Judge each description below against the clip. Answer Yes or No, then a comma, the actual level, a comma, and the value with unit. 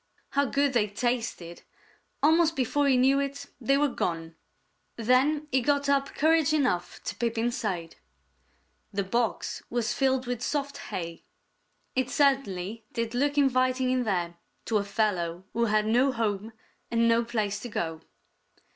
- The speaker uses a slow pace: No, average, 150 wpm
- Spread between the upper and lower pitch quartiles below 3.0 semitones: No, average, 4.8 semitones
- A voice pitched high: Yes, high, 240 Hz